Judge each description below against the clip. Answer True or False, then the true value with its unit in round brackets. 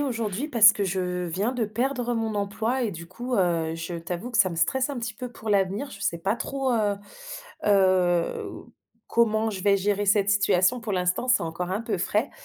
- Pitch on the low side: False (205 Hz)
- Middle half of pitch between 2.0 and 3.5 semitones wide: False (4.2 semitones)